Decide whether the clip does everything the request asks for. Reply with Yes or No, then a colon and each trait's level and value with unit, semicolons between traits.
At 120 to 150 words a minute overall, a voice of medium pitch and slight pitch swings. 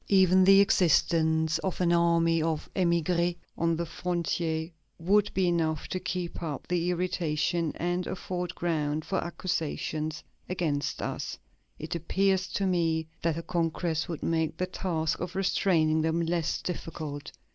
Yes: average, 145 wpm; medium, 170 Hz; narrow, 2.1 semitones